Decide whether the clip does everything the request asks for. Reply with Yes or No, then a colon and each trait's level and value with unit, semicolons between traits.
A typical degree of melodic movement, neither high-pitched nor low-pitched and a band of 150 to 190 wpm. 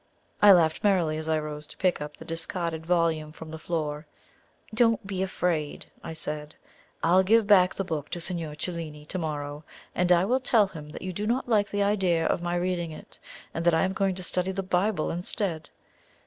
No: average, 3.3 semitones; medium, 175 Hz; fast, 205 wpm